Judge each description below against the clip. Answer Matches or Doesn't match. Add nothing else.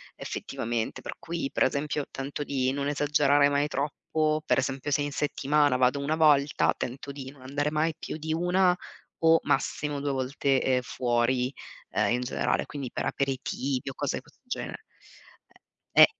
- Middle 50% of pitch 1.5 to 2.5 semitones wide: Matches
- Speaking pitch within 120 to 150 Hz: Matches